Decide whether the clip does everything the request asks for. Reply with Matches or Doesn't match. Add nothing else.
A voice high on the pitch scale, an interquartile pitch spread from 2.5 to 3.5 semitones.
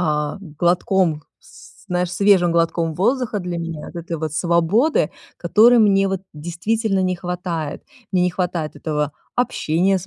Doesn't match